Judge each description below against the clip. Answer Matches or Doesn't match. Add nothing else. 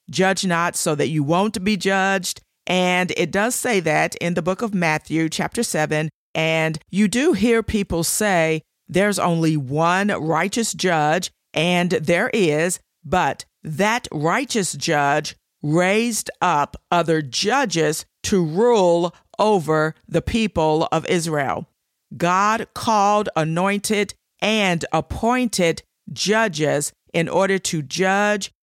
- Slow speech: Matches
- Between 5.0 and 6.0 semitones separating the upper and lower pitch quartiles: Doesn't match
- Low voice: Doesn't match